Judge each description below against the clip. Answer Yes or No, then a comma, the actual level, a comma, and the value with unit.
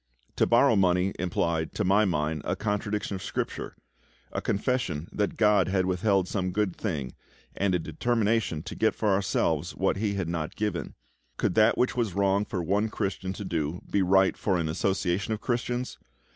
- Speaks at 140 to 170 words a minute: No, average, 180 wpm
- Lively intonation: No, average, 3.1 semitones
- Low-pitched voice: Yes, very low, 95 Hz